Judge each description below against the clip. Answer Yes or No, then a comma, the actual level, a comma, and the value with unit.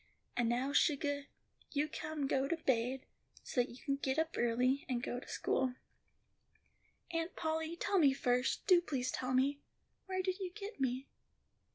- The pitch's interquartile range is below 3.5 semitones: No, average, 4.0 semitones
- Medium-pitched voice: No, very high, 275 Hz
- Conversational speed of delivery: Yes, average, 165 wpm